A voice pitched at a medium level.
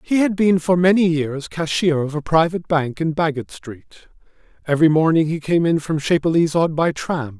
Yes: medium, 160 Hz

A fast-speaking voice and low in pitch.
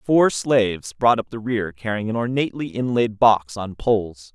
No: average, 180 wpm; low, 110 Hz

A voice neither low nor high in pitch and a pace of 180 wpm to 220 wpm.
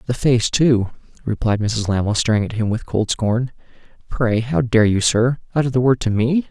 No: low, 115 Hz; fast, 205 wpm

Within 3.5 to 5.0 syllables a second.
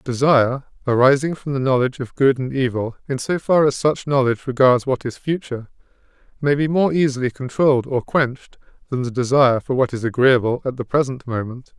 No: 5.8 syllables/s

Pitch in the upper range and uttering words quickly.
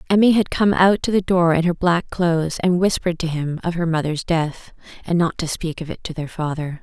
No: medium, 170 Hz; fast, 245 wpm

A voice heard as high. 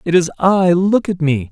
No: medium, 175 Hz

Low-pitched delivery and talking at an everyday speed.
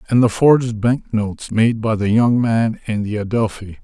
Yes: low, 110 Hz; average, 190 wpm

